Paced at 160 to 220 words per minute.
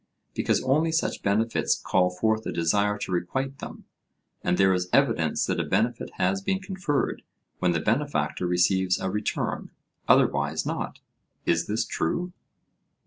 No: average, 145 wpm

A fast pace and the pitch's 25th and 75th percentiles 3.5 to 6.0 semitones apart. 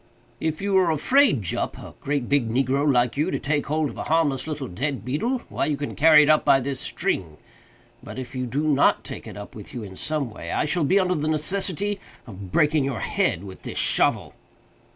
Yes: fast, 215 wpm; average, 4.0 semitones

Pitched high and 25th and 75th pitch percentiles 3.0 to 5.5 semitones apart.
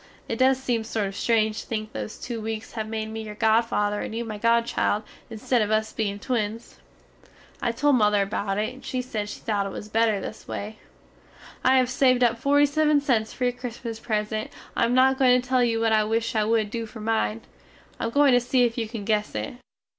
No: high, 225 Hz; narrow, 2.5 semitones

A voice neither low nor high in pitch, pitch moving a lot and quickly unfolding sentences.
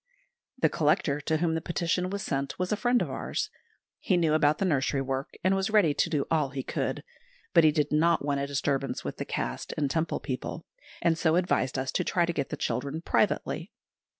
No: medium, 155 Hz; average, 3.5 semitones; fast, 215 wpm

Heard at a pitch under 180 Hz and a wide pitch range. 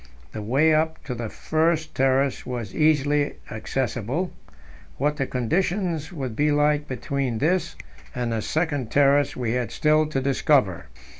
No: medium, 140 Hz; average, 3.8 semitones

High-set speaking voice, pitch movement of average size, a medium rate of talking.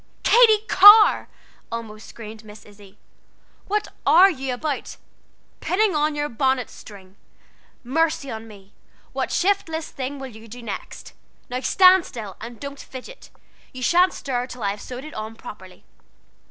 No: very high, 255 Hz; wide, 6.8 semitones; average, 150 wpm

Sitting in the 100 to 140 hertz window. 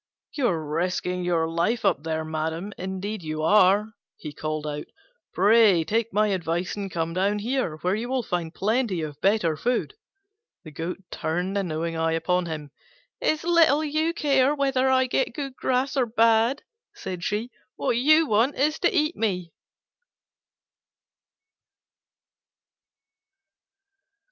No: high, 200 Hz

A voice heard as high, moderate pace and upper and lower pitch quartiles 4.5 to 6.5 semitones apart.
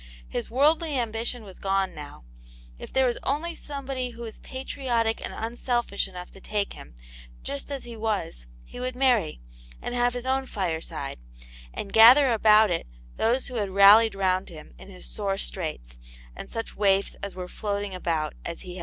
Yes: high, 215 Hz; average, 180 wpm; average, 4.8 semitones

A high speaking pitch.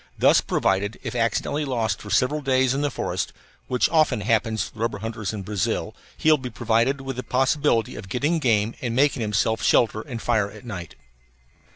No: low, 115 Hz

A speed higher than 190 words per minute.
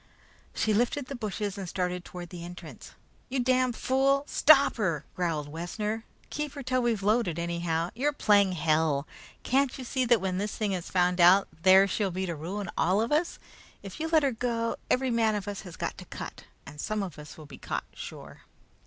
Yes: fast, 205 wpm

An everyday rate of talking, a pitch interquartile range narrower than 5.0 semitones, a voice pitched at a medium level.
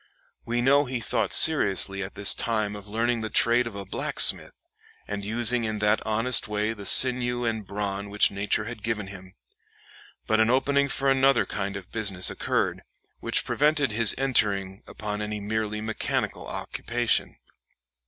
No: average, 160 wpm; average, 3.0 semitones; low, 110 Hz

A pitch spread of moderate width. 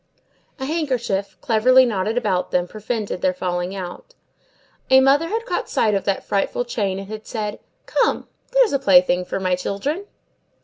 No: wide, 5.7 semitones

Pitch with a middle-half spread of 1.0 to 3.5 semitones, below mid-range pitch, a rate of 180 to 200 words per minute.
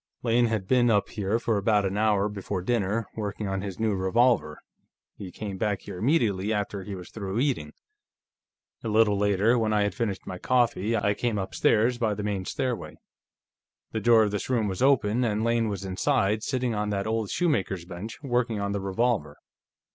Yes: average, 2.9 semitones; low, 105 Hz; average, 190 wpm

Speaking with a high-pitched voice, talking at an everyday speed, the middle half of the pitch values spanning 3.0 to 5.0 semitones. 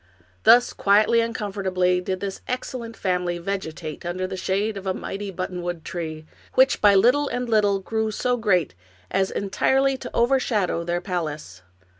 Yes: high, 195 Hz; average, 155 wpm; average, 3.9 semitones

